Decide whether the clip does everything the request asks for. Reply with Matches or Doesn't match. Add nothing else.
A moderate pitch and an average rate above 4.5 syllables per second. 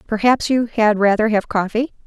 Doesn't match